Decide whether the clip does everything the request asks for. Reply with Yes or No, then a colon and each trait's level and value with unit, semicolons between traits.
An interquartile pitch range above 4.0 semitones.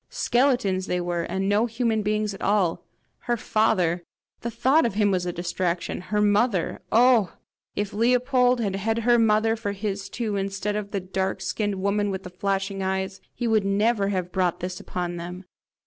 No: average, 2.9 semitones